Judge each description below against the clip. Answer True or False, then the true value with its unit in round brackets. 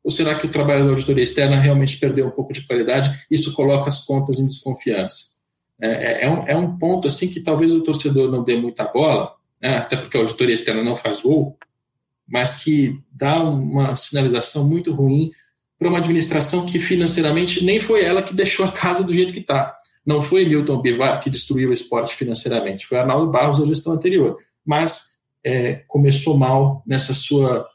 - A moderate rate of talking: False (190 wpm)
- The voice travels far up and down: False (3.5 semitones)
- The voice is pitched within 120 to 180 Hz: True (140 Hz)